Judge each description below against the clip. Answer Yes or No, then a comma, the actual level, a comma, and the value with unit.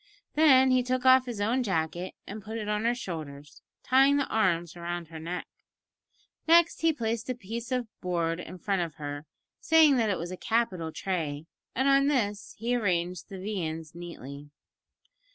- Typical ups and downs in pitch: No, wide, 6.7 semitones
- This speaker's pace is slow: No, average, 175 wpm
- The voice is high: Yes, high, 200 Hz